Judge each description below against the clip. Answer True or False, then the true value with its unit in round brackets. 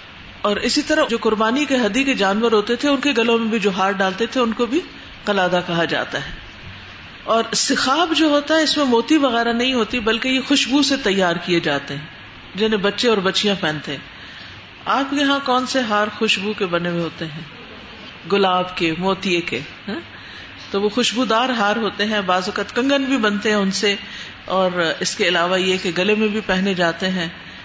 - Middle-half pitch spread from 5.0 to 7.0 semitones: True (5.3 semitones)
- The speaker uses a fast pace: True (205 wpm)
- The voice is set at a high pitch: True (205 Hz)